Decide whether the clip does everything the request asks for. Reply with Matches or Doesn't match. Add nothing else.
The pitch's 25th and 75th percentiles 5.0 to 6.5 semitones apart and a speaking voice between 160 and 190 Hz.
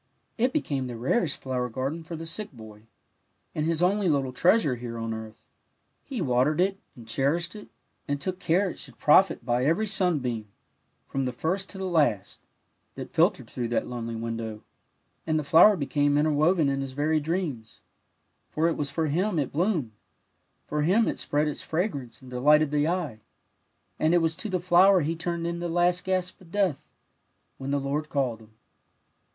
Doesn't match